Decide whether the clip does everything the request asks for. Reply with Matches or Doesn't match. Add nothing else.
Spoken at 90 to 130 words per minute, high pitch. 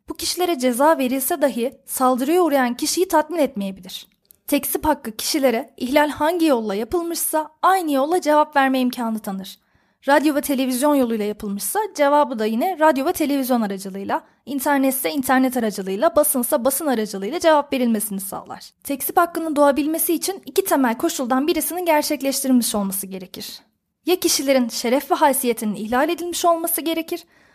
Doesn't match